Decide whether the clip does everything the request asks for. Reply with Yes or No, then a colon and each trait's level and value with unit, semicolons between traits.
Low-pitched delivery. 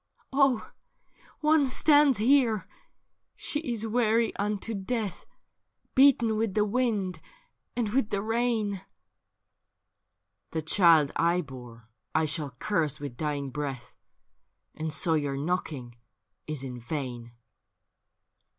No: high, 190 Hz